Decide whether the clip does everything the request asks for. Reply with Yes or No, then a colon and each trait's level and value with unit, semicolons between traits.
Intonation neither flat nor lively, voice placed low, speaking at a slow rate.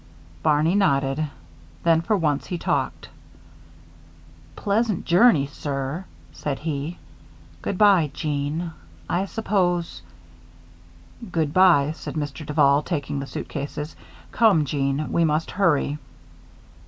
No: average, 3.8 semitones; medium, 155 Hz; slow, 110 wpm